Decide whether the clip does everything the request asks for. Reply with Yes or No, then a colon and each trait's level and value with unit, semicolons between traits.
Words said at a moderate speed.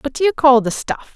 No: fast, 260 wpm